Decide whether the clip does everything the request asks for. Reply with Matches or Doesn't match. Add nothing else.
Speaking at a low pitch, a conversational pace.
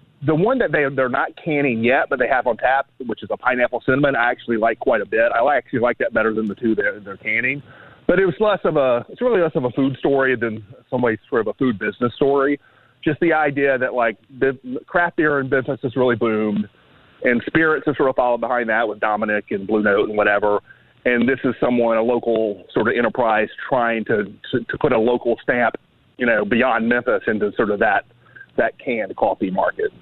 Doesn't match